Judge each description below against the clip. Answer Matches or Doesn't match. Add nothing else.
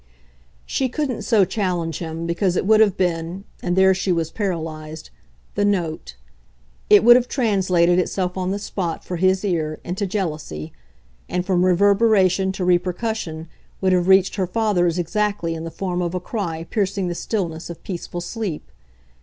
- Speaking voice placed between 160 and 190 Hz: Matches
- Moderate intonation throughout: Matches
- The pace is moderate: Matches